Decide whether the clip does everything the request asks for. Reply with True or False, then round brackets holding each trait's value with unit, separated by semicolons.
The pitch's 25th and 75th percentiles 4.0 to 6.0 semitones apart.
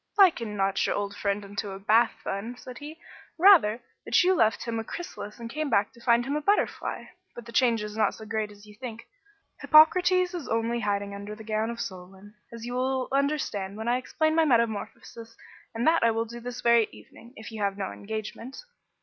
False (3.6 semitones)